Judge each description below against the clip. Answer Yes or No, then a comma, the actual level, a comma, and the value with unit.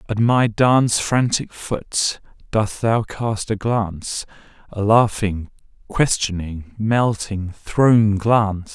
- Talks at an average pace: No, slow, 110 wpm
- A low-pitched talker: Yes, low, 105 Hz